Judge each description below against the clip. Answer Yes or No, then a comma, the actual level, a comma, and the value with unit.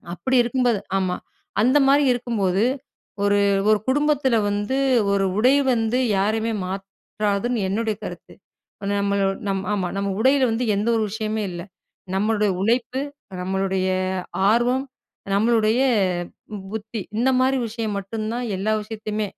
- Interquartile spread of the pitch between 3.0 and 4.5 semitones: Yes, average, 3.3 semitones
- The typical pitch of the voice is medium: No, high, 220 Hz